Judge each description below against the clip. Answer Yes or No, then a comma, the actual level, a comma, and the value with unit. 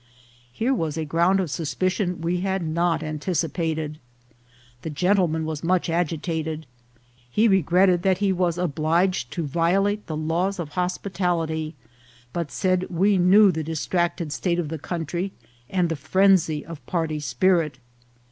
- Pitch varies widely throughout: No, narrow, 2.6 semitones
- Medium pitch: Yes, medium, 170 Hz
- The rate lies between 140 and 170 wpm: Yes, average, 145 wpm